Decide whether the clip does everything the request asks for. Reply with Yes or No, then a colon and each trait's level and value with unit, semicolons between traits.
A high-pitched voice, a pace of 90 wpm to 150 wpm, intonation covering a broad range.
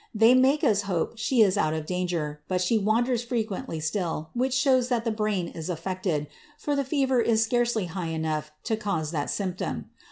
No: high, 205 Hz; average, 190 wpm; wide, 6.3 semitones